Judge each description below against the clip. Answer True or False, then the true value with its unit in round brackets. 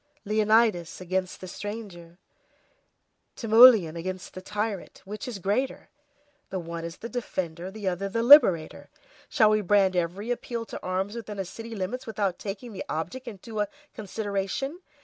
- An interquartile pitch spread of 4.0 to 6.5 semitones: False (3.5 semitones)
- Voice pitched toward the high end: True (200 Hz)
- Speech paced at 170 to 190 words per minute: False (155 wpm)